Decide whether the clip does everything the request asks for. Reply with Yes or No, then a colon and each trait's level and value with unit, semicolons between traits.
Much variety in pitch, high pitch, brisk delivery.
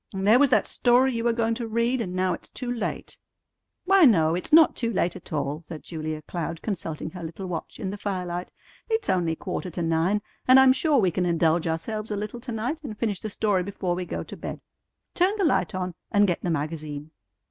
Yes: wide, 5.7 semitones; high, 195 Hz; fast, 225 wpm